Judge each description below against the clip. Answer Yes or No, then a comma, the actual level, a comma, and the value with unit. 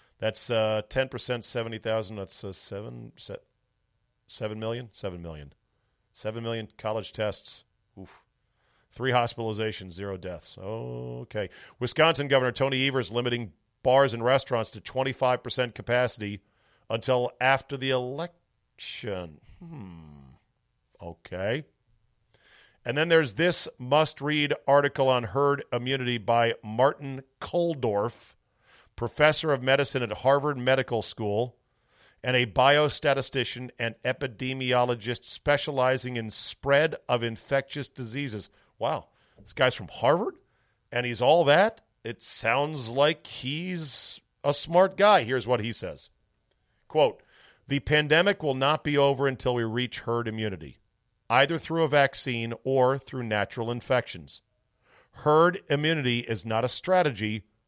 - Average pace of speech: No, slow, 120 wpm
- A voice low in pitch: Yes, low, 125 Hz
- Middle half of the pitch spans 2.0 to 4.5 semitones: Yes, average, 3.8 semitones